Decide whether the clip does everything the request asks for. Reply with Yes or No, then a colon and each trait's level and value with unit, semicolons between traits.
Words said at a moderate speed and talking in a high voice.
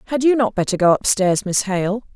No: fast, 225 wpm; high, 205 Hz